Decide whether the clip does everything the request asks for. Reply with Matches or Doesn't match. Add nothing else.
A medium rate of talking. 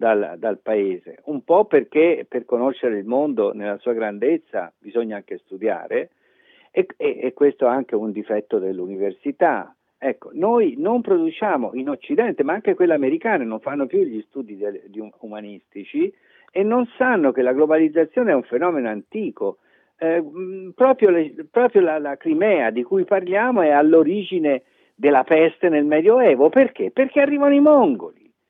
Matches